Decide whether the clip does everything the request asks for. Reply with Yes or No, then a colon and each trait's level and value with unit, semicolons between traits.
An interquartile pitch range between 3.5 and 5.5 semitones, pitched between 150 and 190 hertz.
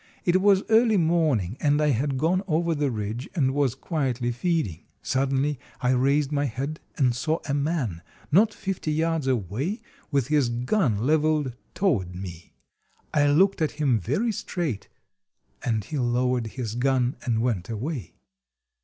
No: average, 4.7 semitones; medium, 140 Hz